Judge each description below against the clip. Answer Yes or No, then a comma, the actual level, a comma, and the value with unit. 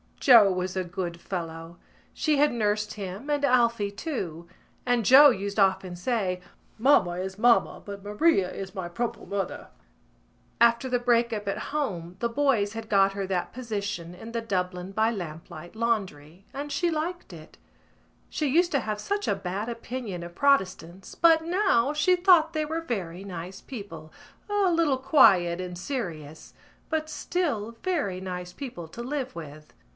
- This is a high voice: Yes, high, 210 Hz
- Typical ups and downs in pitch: No, wide, 6.9 semitones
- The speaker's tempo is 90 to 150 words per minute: No, average, 160 wpm